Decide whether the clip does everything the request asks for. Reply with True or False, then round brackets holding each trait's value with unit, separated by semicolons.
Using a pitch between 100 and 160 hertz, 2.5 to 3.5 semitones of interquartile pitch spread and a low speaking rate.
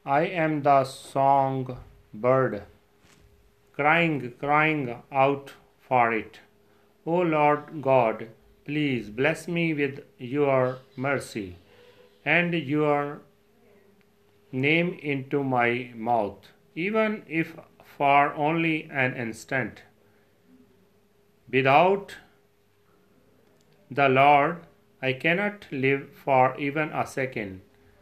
False (140 Hz; 4.5 semitones; 90 wpm)